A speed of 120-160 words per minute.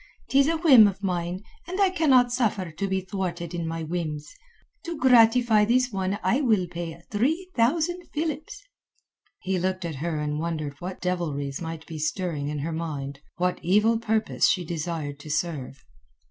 No: average, 170 wpm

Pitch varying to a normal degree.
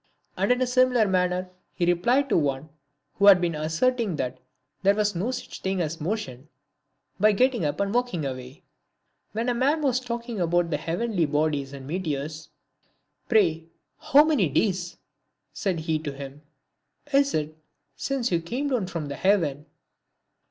No: wide, 7.2 semitones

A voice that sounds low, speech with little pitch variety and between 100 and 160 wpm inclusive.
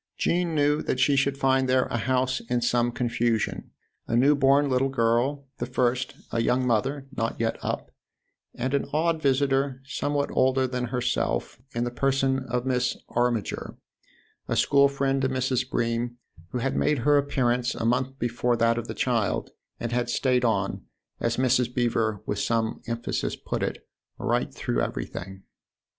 No: low, 125 Hz; narrow, 2.3 semitones; average, 180 wpm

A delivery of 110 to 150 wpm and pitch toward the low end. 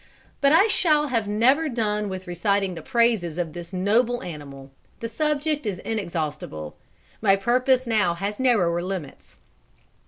No: average, 145 wpm; high, 210 Hz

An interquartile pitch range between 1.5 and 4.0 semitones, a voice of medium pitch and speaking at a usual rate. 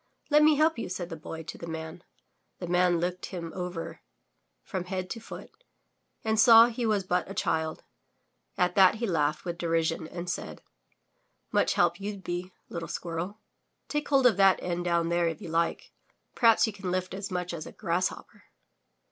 Yes: average, 3.0 semitones; medium, 180 Hz; average, 190 wpm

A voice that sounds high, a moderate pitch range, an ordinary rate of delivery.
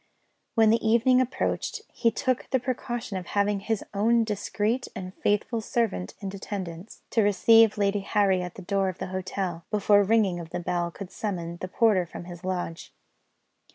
Yes: high, 200 Hz; average, 3.6 semitones; average, 180 wpm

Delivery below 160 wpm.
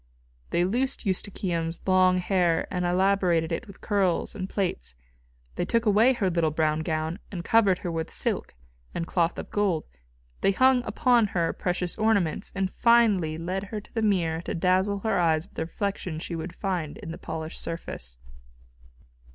No: average, 170 wpm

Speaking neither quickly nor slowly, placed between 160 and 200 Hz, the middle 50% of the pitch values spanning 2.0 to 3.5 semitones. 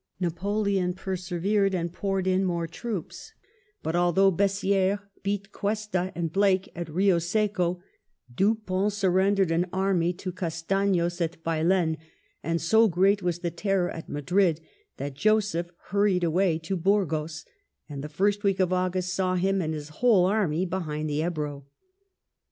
Yes: average, 145 wpm; medium, 185 Hz; average, 2.8 semitones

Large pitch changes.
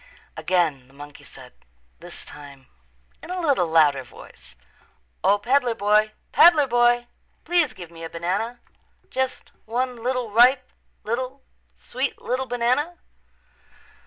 Yes: wide, 7.2 semitones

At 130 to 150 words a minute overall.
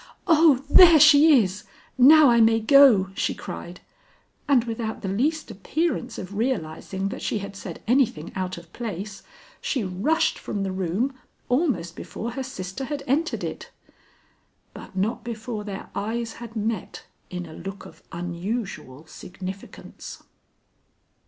Yes: average, 140 wpm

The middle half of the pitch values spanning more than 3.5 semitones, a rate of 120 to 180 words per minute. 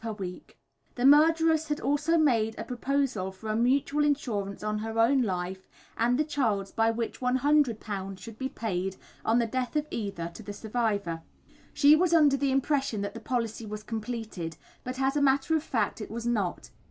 No: average, 4.8 semitones; average, 190 wpm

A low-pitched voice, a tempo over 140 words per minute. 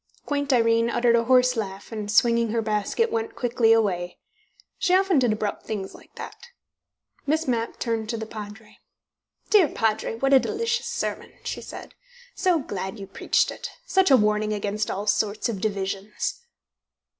No: high, 225 Hz; average, 165 wpm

